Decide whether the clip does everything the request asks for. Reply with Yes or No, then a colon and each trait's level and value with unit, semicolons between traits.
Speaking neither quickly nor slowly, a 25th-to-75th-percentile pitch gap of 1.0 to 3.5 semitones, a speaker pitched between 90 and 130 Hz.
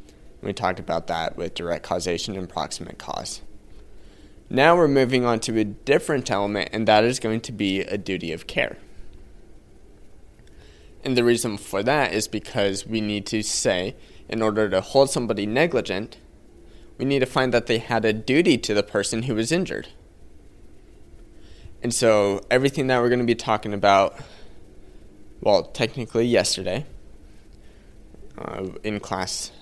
Yes: average, 155 wpm; average, 3.2 semitones; low, 110 Hz